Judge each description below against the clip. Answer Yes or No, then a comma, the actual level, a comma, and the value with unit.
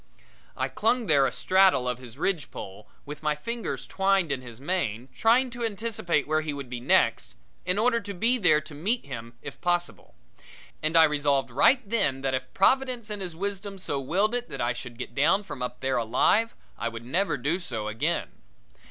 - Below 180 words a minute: No, average, 195 wpm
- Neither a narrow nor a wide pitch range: No, wide, 7.6 semitones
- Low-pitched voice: No, medium, 155 Hz